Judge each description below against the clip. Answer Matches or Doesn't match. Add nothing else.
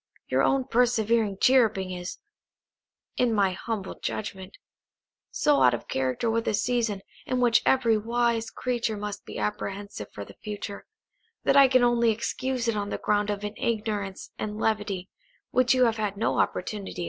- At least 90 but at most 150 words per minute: Doesn't match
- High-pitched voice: Matches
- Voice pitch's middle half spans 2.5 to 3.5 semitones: Matches